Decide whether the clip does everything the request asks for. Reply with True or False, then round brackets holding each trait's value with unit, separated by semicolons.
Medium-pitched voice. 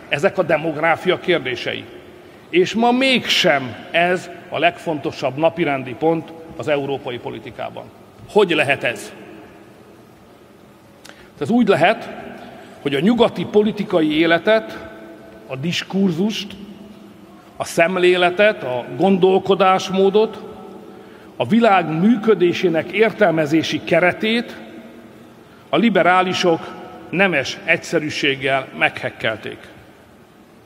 True (175 Hz)